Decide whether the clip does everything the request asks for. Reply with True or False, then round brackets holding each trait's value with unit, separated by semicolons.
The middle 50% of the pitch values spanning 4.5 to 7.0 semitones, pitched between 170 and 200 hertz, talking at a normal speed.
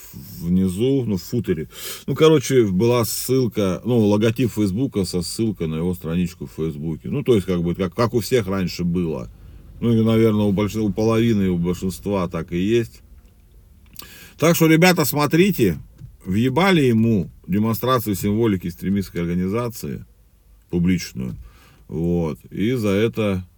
False (5.1 semitones; 105 Hz; 145 wpm)